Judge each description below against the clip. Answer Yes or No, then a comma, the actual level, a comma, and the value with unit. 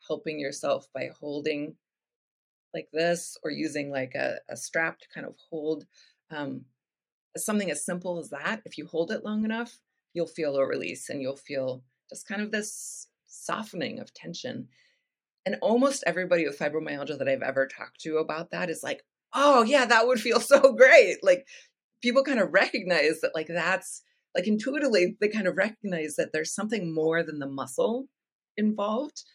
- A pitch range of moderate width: No, wide, 7.7 semitones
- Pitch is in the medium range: Yes, medium, 180 Hz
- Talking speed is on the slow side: No, average, 175 wpm